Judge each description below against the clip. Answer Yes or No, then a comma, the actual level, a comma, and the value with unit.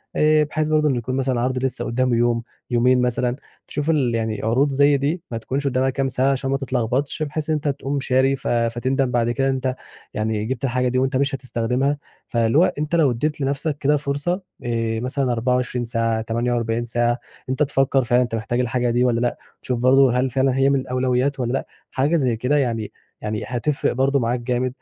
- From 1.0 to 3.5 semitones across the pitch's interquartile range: Yes, narrow, 2.5 semitones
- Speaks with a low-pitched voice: Yes, low, 130 Hz